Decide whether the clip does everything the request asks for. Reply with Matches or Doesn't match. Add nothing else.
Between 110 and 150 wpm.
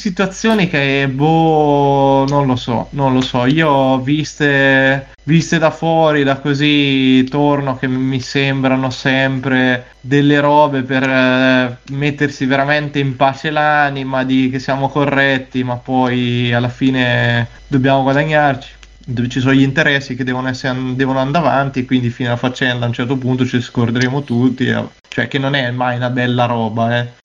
Doesn't match